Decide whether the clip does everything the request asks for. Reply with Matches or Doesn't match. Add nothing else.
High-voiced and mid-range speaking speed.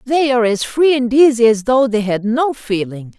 Doesn't match